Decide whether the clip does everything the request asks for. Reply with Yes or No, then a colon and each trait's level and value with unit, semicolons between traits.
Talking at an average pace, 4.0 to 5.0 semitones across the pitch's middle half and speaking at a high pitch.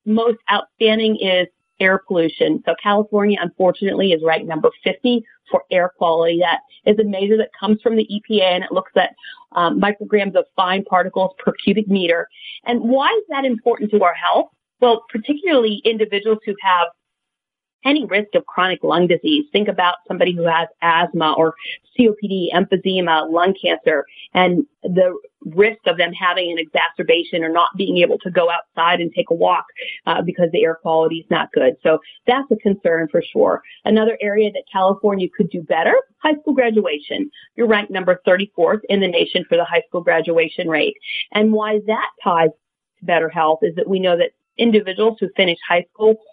Yes: average, 180 wpm; average, 4.3 semitones; high, 195 Hz